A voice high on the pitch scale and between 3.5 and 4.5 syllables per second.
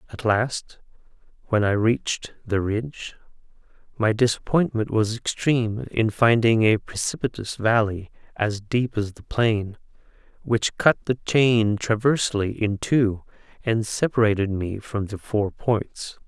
No: low, 110 Hz; 4.1 syllables/s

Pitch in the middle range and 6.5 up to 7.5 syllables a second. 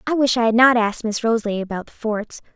No: high, 230 Hz; 6.6 syllables/s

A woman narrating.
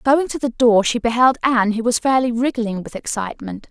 Yes: female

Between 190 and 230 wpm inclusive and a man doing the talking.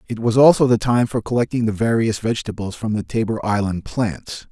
Yes: average, 200 wpm; male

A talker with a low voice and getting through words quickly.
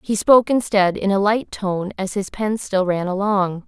No: high, 200 Hz; fast, 215 wpm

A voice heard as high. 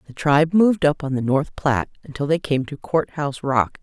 No: medium, 145 Hz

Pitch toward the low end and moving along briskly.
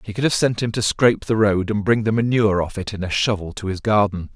Yes: low, 105 Hz; fast, 290 wpm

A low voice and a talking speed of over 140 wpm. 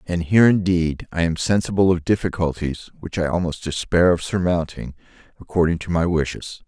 Yes: very low, 85 Hz; average, 160 wpm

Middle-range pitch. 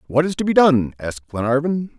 Yes: medium, 145 Hz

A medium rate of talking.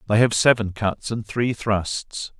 Yes: average, 175 wpm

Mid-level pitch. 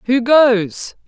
No: high, 240 Hz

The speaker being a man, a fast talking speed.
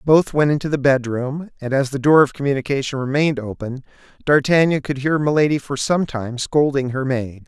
No: male; average, 185 wpm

